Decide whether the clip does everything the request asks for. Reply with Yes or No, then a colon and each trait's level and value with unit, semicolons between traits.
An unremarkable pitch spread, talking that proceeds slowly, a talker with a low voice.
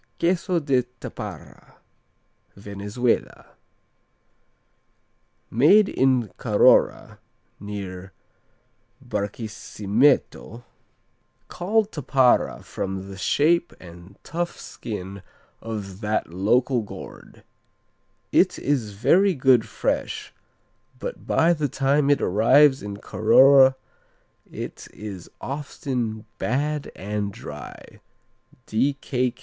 No: wide, 6.0 semitones; slow, 80 wpm; low, 120 Hz